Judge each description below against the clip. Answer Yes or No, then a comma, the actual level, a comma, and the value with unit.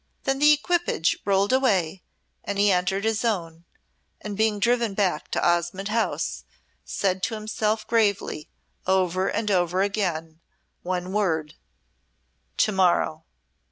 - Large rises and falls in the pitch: No, average, 3.4 semitones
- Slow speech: Yes, slow, 125 wpm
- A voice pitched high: Yes, high, 195 Hz